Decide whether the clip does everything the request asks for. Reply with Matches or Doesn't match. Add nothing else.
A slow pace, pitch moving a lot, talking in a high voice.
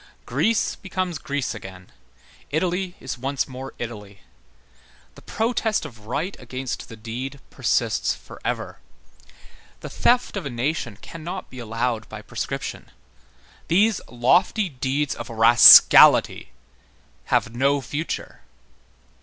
Doesn't match